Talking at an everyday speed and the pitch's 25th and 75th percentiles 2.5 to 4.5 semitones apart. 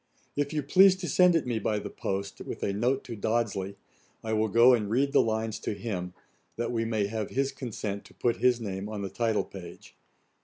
No: fast, 220 wpm; average, 3.8 semitones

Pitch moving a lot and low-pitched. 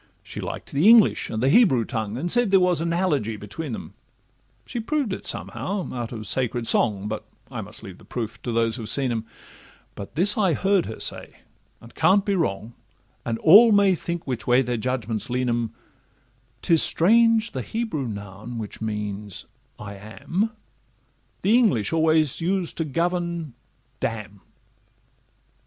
Yes: wide, 8.6 semitones; low, 130 Hz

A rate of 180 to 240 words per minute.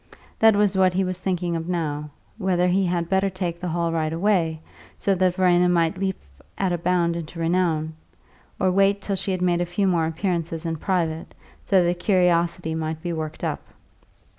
Yes: average, 190 wpm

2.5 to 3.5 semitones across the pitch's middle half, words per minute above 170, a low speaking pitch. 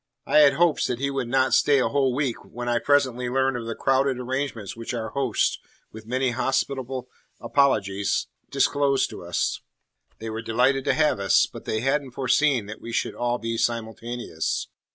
Yes: average, 2.8 semitones; average, 180 wpm; low, 125 Hz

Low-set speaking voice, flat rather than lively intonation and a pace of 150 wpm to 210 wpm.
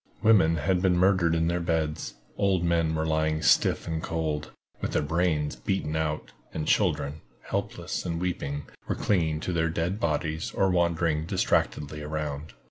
Yes: very low, 80 Hz; narrow, 2.2 semitones; average, 160 wpm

